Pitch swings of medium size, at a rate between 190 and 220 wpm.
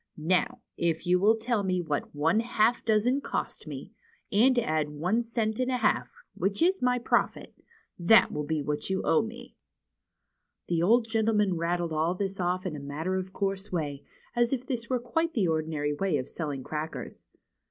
No: wide, 6.1 semitones; average, 195 wpm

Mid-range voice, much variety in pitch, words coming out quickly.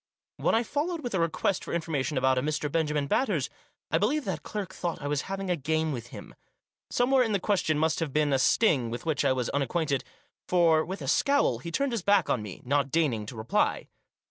Yes: medium, 160 Hz; wide, 5.9 semitones; fast, 220 wpm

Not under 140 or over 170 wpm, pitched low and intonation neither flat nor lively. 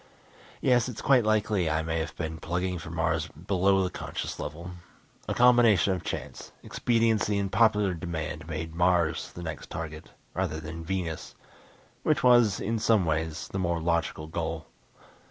Yes: average, 155 wpm; very low, 85 Hz; average, 4.2 semitones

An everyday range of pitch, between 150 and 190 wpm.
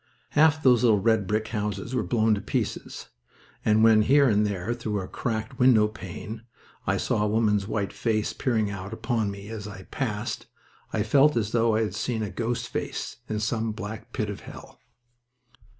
No: narrow, 2.0 semitones; average, 185 wpm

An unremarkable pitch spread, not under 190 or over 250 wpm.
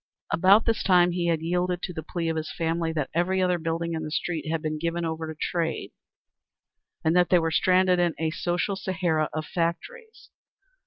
No: narrow, 1.9 semitones; average, 200 wpm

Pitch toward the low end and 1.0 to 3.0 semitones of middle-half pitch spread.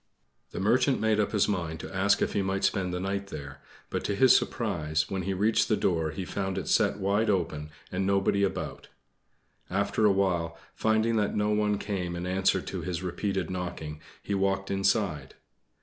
Yes: very low, 95 Hz; narrow, 2.5 semitones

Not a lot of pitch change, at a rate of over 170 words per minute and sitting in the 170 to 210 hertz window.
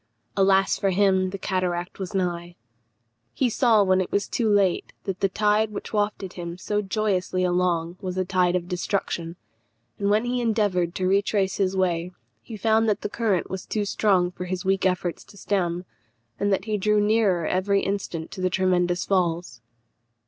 Yes: narrow, 2.3 semitones; average, 180 wpm; high, 190 Hz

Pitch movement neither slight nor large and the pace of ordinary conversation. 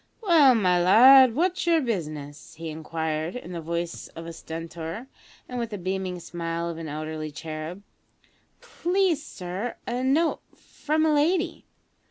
No: wide, 8.5 semitones; average, 150 wpm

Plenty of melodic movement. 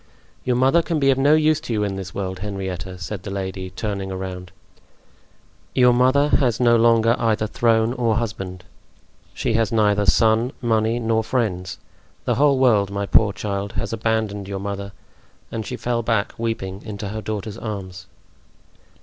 No: average, 3.2 semitones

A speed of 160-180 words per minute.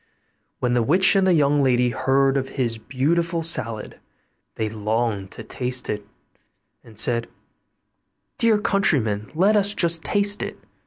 No: average, 145 wpm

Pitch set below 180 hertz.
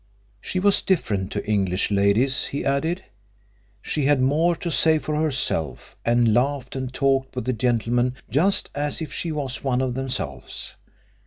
Yes: low, 135 Hz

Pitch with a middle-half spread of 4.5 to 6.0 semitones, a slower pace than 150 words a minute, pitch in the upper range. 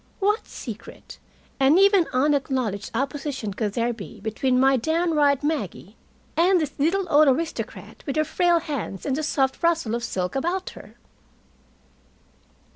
Yes: average, 5.2 semitones; average, 140 wpm; very high, 280 Hz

